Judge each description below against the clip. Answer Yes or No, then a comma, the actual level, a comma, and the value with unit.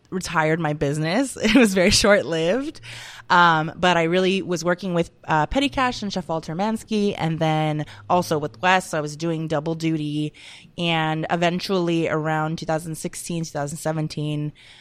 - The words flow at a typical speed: Yes, average, 150 wpm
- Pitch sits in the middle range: Yes, medium, 165 Hz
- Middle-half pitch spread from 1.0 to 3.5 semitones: Yes, average, 2.9 semitones